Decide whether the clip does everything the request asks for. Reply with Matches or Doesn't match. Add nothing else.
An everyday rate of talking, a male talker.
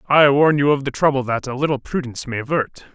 Doesn't match